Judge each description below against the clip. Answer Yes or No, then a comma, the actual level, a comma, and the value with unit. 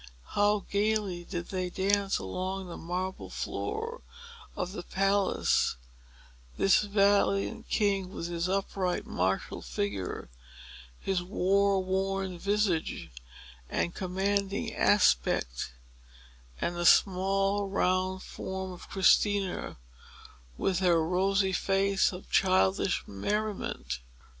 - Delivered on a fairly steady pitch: Yes, narrow, 1.8 semitones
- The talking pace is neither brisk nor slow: No, slow, 100 wpm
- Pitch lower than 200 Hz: Yes, high, 190 Hz